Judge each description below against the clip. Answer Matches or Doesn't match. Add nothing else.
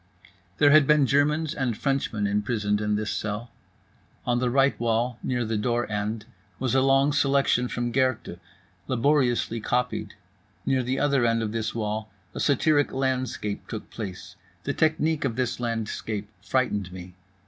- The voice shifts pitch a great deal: Doesn't match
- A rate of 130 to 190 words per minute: Matches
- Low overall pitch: Matches